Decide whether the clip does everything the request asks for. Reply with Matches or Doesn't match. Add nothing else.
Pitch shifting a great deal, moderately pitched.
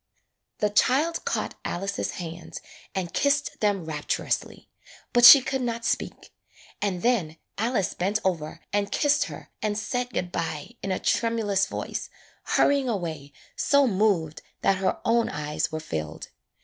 Doesn't match